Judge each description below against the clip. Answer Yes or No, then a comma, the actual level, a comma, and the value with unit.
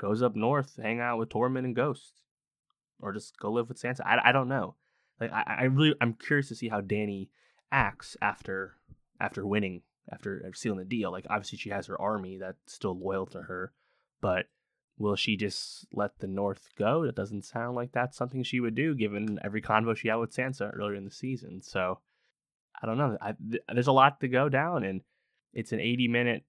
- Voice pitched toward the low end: Yes, low, 115 Hz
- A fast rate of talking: Yes, fast, 210 wpm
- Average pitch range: Yes, average, 3.7 semitones